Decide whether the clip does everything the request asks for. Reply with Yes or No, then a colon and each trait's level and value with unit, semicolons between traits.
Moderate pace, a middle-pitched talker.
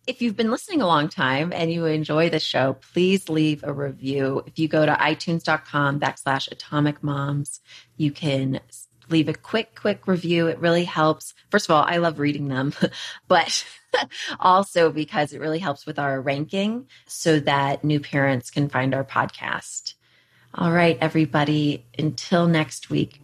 Yes: average, 165 wpm; medium, 150 Hz